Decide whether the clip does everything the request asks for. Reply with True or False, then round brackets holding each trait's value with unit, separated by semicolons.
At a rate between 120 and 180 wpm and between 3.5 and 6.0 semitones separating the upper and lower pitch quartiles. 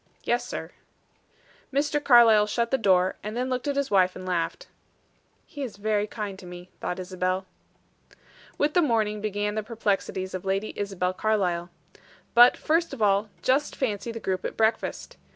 True (170 wpm; 4.3 semitones)